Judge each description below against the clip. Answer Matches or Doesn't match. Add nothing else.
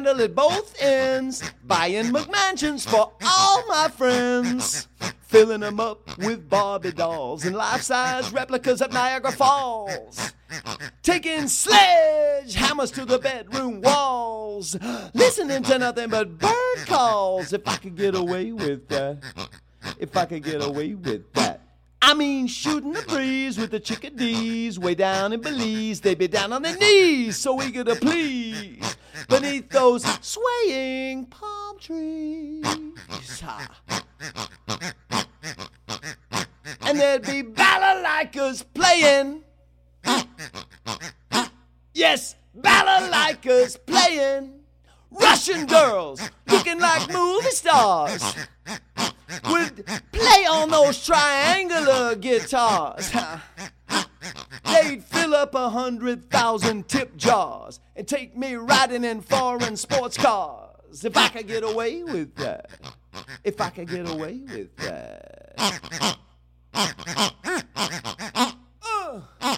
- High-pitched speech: Matches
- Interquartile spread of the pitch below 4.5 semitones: Doesn't match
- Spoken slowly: Matches